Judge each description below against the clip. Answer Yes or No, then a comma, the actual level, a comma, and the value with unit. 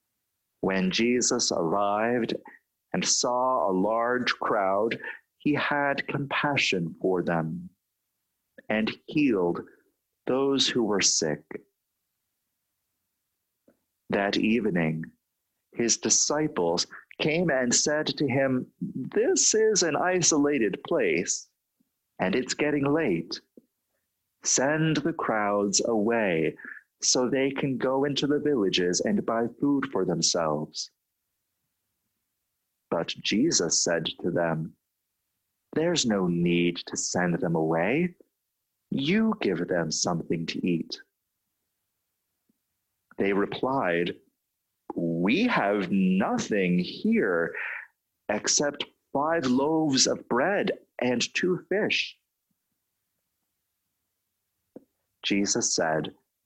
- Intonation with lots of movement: Yes, wide, 7.9 semitones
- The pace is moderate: No, slow, 90 wpm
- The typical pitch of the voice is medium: No, low, 110 Hz